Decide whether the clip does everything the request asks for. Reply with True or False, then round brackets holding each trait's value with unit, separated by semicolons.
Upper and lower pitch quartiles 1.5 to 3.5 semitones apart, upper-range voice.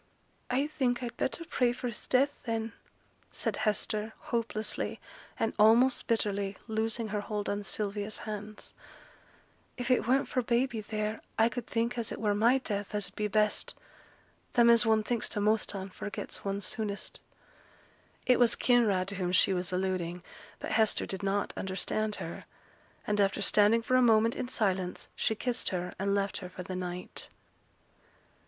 True (2.9 semitones; 215 Hz)